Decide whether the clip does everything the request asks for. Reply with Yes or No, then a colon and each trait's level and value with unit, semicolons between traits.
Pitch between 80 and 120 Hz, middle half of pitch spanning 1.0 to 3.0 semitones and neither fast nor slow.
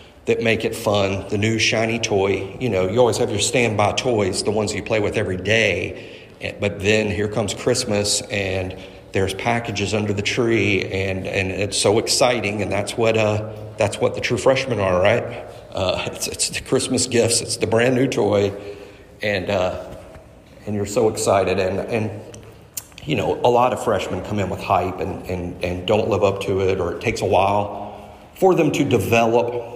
Yes: low, 105 Hz; average, 2.7 semitones; average, 190 wpm